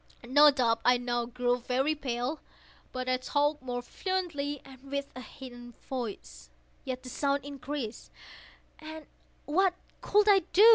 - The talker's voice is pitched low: No, very high, 265 Hz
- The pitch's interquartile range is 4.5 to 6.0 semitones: No, average, 3.1 semitones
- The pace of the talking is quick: No, slow, 135 wpm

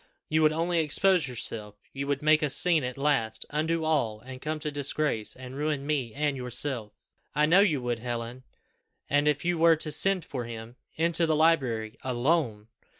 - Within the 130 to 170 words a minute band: No, average, 185 wpm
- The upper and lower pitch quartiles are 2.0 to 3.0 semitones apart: No, average, 4.3 semitones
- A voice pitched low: No, medium, 145 Hz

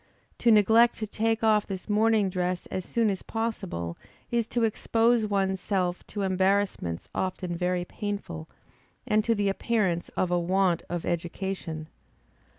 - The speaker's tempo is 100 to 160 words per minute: Yes, average, 150 wpm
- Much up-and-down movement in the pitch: No, average, 3.5 semitones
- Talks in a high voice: Yes, high, 195 Hz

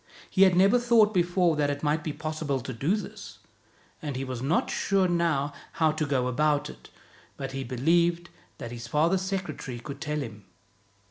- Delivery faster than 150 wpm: Yes, average, 185 wpm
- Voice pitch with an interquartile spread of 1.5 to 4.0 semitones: No, average, 4.4 semitones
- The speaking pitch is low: No, medium, 155 Hz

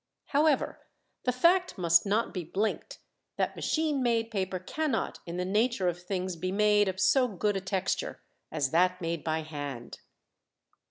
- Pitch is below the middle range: No, high, 190 Hz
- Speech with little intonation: No, average, 4.7 semitones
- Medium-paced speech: Yes, average, 160 wpm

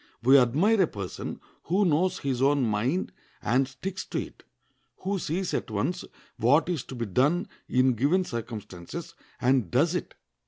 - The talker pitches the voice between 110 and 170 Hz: Yes, low, 135 Hz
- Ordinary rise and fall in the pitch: No, wide, 6.7 semitones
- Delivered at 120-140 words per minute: No, average, 160 wpm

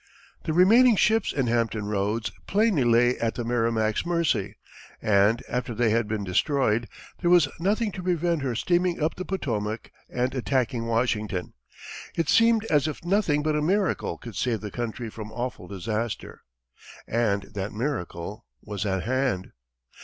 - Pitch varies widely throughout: Yes, wide, 7.3 semitones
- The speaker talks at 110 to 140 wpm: No, average, 155 wpm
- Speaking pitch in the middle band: No, low, 120 Hz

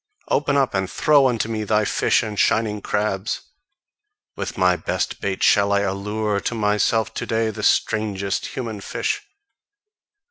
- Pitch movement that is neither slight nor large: No, narrow, 2.1 semitones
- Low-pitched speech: Yes, low, 105 Hz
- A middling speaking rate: Yes, average, 150 wpm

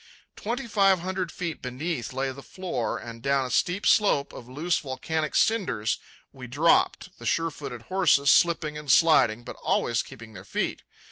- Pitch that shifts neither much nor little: No, wide, 5.9 semitones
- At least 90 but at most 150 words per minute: No, average, 165 wpm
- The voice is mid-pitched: Yes, medium, 145 Hz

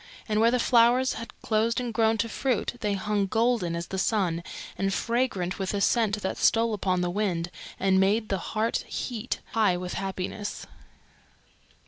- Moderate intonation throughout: Yes, average, 3.4 semitones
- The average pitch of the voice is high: Yes, high, 210 Hz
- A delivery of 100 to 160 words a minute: No, average, 170 wpm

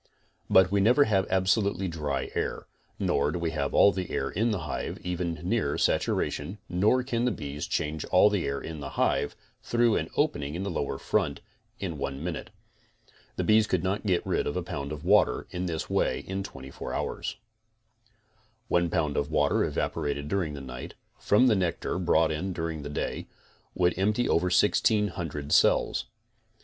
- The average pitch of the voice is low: Yes, very low, 90 Hz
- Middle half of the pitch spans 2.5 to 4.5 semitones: No, average, 4.9 semitones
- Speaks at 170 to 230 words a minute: Yes, average, 180 wpm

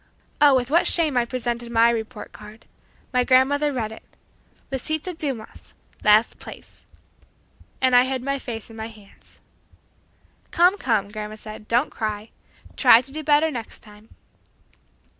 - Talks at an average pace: Yes, average, 145 wpm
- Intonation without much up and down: No, average, 4.0 semitones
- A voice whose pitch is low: No, high, 245 Hz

